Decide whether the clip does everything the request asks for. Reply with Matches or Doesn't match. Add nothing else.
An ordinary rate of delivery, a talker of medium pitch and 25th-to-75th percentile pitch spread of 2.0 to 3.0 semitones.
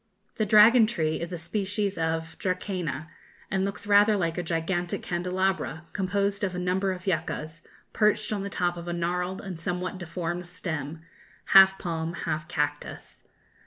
Matches